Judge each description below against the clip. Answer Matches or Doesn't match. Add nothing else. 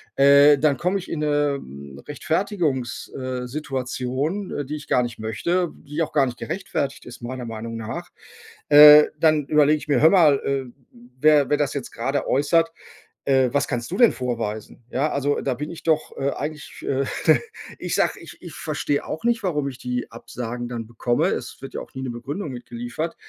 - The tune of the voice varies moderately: Matches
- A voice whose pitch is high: Doesn't match